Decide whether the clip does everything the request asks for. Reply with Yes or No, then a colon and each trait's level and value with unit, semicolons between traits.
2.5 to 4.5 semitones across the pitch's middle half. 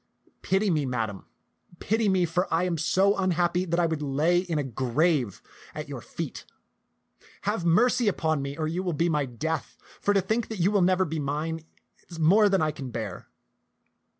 Yes: average, 3.9 semitones